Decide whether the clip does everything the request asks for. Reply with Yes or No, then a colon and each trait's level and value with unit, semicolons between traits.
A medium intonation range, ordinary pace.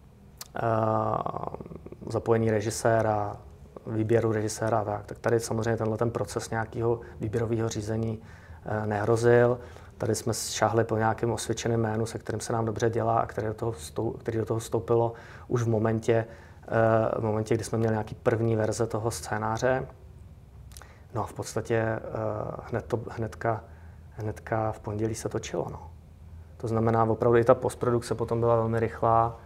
No: narrow, 1.3 semitones; average, 155 wpm